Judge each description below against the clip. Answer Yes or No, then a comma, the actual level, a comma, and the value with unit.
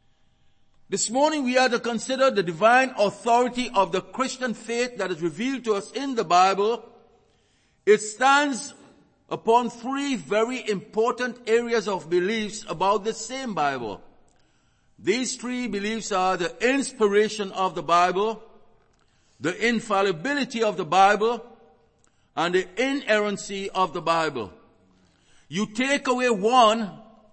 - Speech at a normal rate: No, slow, 125 wpm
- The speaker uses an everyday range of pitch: Yes, average, 4.2 semitones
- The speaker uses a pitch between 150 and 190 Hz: No, high, 220 Hz